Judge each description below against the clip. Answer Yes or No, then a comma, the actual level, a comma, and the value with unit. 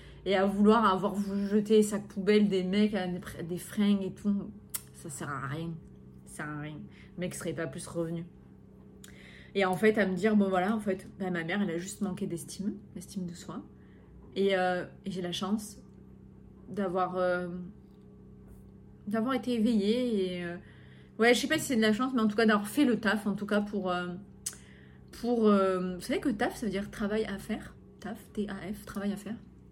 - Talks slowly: No, average, 205 wpm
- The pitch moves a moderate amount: Yes, average, 3.0 semitones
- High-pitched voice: Yes, high, 195 Hz